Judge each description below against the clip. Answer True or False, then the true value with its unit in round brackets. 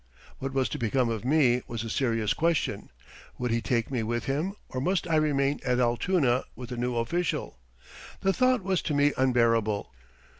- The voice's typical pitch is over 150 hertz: False (130 Hz)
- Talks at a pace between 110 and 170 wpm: False (185 wpm)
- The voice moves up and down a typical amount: True (4.6 semitones)